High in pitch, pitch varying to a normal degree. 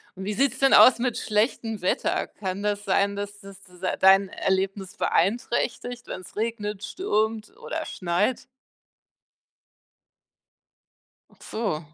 Yes: high, 205 Hz; average, 3.0 semitones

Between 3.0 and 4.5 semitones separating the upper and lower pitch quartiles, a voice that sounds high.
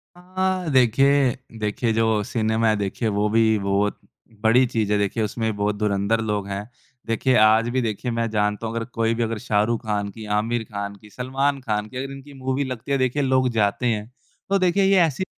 No: average, 3.7 semitones; low, 115 Hz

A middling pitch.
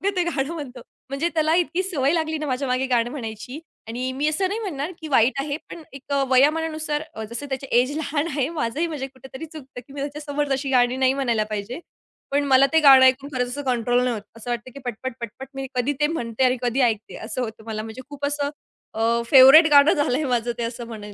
No: very high, 270 Hz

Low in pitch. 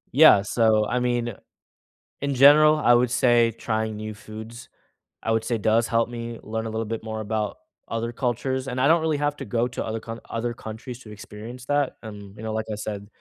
Yes: low, 115 Hz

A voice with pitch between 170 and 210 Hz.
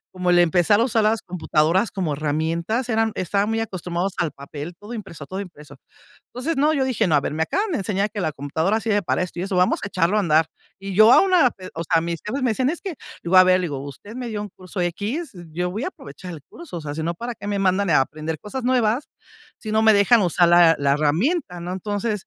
Yes: high, 190 Hz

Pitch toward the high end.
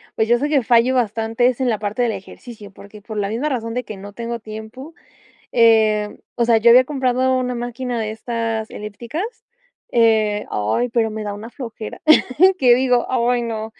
Yes: high, 230 Hz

